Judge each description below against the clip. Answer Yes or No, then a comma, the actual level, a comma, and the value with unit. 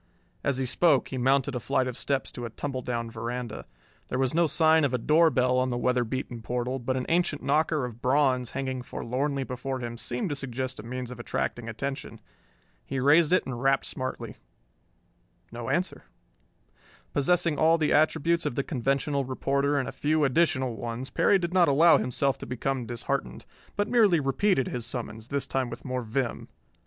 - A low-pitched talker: Yes, low, 130 Hz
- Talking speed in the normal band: Yes, average, 185 wpm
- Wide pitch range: No, average, 2.8 semitones